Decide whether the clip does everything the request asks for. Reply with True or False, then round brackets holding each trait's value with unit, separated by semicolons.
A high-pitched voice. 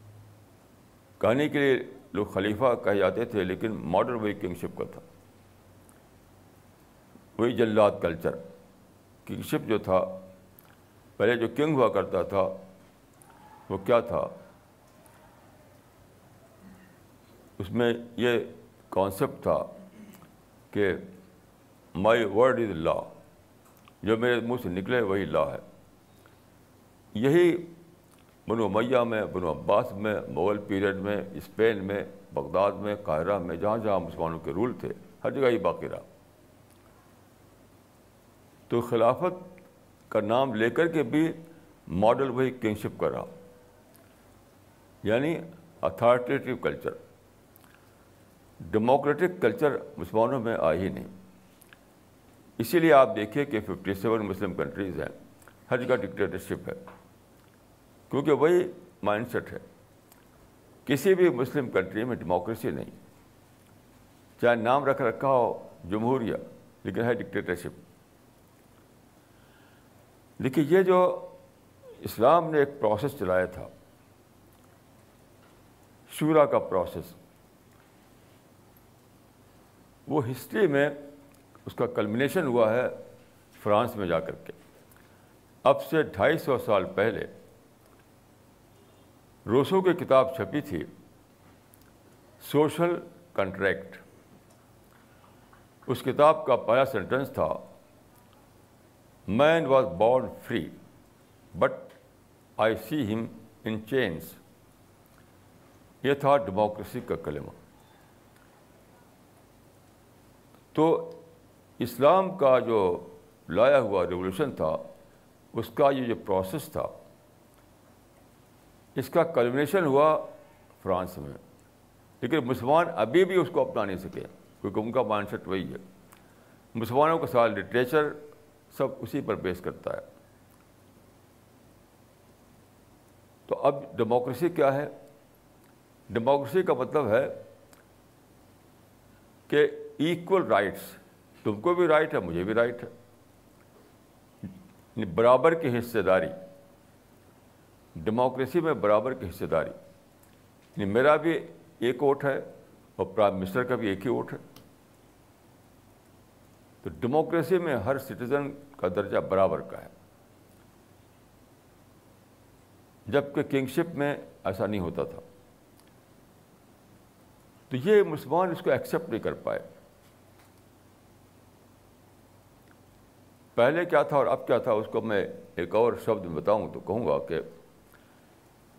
False (120 Hz)